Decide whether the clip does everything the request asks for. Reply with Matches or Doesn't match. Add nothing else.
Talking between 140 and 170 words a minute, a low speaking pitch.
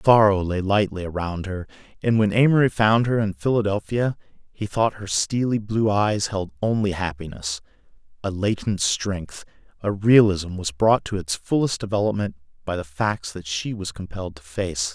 Matches